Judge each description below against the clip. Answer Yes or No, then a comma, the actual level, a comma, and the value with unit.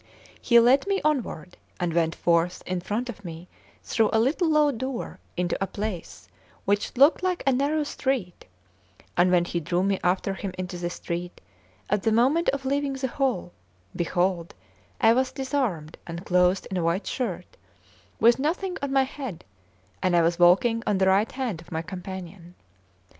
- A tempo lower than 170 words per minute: No, average, 175 wpm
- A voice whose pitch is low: No, high, 200 Hz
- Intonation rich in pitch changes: Yes, wide, 7.0 semitones